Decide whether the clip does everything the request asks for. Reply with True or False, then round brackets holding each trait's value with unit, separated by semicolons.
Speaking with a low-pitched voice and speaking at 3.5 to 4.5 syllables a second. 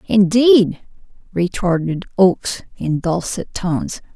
False (190 Hz; 3.7 syllables/s)